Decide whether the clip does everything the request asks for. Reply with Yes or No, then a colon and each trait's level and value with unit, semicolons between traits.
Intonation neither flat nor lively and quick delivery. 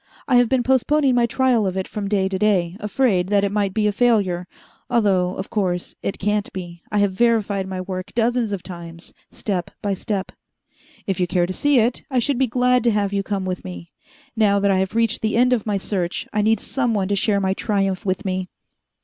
Yes: average, 3.5 semitones; fast, 225 wpm